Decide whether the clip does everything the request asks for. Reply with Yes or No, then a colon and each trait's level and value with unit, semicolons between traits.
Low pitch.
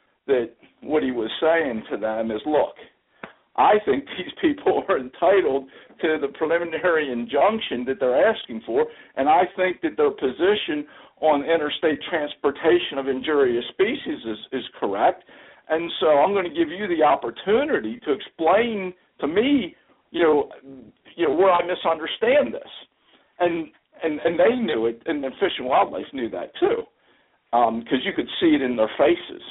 No: medium, 170 Hz